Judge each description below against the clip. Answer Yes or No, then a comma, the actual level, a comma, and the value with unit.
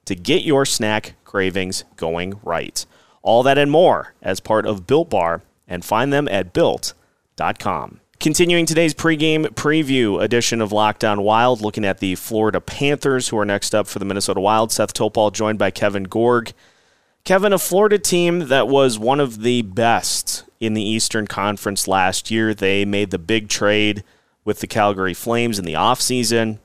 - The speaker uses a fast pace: No, average, 170 wpm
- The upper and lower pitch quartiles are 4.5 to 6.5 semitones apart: Yes, average, 4.8 semitones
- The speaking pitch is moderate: No, low, 110 Hz